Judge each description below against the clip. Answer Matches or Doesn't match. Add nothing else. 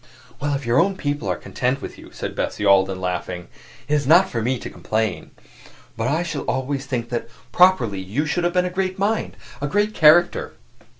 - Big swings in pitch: Matches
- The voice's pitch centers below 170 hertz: Matches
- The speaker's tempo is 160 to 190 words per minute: Doesn't match